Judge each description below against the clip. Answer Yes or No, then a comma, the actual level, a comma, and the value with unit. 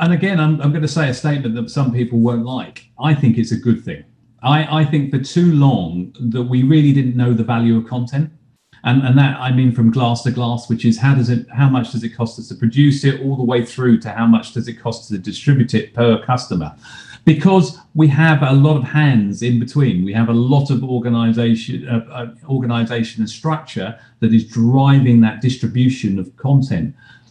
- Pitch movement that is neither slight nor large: Yes, average, 3.1 semitones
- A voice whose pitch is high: No, low, 125 Hz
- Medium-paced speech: No, fast, 220 wpm